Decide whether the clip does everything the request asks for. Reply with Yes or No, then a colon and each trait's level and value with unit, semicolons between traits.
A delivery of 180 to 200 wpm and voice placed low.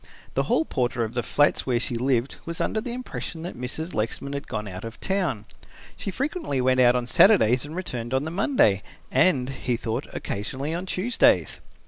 Yes: average, 190 wpm; low, 130 Hz